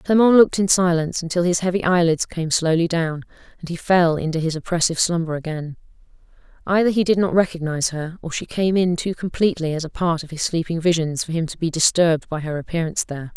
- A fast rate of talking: Yes, fast, 210 wpm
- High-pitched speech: No, medium, 170 Hz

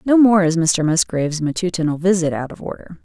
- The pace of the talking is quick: No, average, 195 wpm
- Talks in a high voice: No, medium, 175 Hz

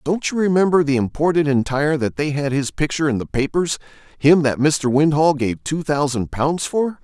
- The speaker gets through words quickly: No, average, 190 wpm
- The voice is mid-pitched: Yes, medium, 150 Hz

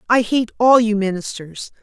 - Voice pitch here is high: Yes, high, 220 Hz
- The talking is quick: No, average, 165 wpm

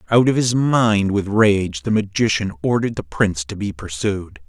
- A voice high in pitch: No, low, 100 Hz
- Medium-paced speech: Yes, average, 190 wpm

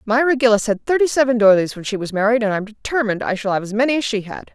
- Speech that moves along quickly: Yes, fast, 275 wpm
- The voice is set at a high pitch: Yes, high, 225 Hz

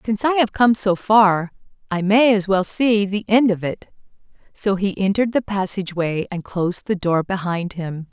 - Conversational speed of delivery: Yes, average, 190 wpm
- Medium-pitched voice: No, high, 195 Hz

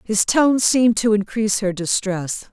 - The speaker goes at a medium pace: Yes, average, 165 wpm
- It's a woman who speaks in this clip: Yes, female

